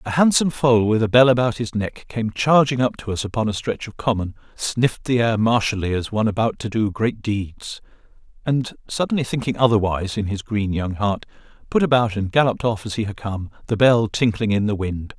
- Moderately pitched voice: No, low, 110 Hz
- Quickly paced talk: Yes, fast, 215 wpm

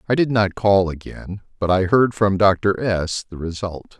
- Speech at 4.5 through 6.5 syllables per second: No, 4.2 syllables/s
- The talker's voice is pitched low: Yes, low, 100 Hz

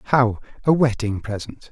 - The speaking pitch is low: Yes, low, 120 Hz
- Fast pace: No, average, 140 wpm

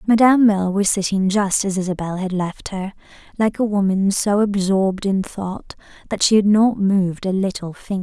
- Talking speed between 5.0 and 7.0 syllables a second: Yes, 5.2 syllables/s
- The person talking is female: Yes, female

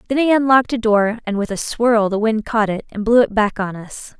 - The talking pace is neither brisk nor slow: No, fast, 270 wpm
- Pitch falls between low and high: No, high, 220 Hz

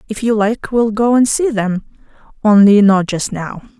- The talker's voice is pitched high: Yes, high, 215 Hz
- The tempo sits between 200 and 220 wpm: No, average, 190 wpm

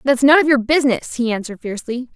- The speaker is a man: No, female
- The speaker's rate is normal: No, fast, 220 wpm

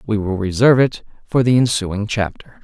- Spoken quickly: No, average, 180 wpm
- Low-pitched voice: Yes, low, 110 Hz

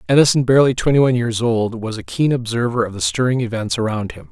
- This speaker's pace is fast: Yes, fast, 220 wpm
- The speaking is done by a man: Yes, male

